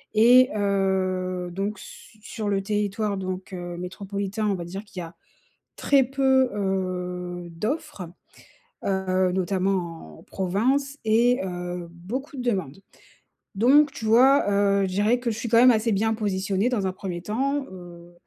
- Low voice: No, high, 200 Hz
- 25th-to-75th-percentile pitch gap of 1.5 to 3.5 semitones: No, average, 4.0 semitones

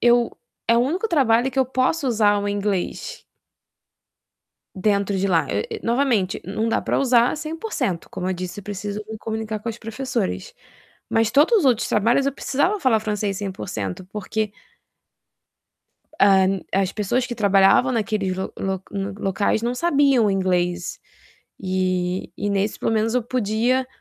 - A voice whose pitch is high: Yes, high, 215 Hz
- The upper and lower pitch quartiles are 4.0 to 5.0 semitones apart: Yes, average, 4.3 semitones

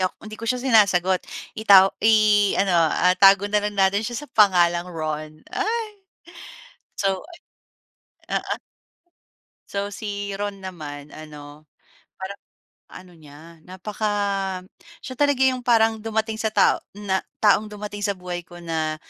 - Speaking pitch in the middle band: No, high, 200 Hz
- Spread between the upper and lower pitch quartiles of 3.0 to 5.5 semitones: Yes, average, 3.4 semitones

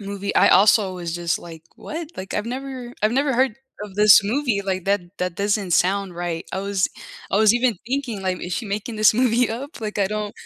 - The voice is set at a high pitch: Yes, high, 205 Hz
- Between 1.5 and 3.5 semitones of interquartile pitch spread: No, average, 3.9 semitones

